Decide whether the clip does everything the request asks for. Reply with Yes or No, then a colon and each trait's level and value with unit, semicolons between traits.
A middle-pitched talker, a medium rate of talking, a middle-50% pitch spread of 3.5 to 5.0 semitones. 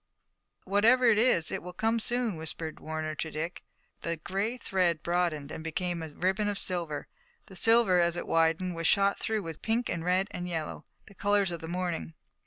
Yes: medium, 180 Hz; average, 190 wpm; average, 3.8 semitones